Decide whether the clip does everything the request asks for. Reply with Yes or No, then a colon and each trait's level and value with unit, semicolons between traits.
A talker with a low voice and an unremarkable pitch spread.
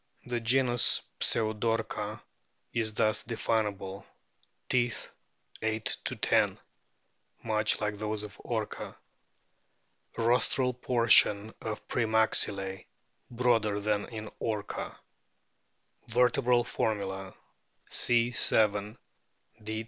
No: low, 110 Hz; narrow, 2.1 semitones